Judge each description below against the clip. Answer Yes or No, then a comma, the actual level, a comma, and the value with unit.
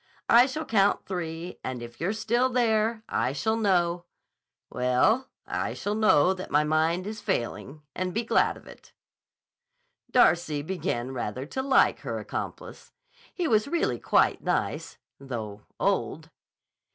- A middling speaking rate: No, slow, 130 wpm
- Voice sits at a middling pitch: Yes, medium, 180 Hz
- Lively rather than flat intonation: Yes, wide, 7.4 semitones